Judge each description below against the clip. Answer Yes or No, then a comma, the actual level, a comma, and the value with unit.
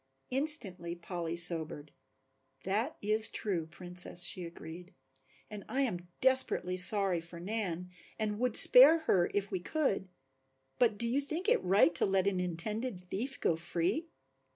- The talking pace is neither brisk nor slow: Yes, average, 150 wpm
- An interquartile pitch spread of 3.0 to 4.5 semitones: No, average, 5.1 semitones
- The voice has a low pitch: No, high, 190 Hz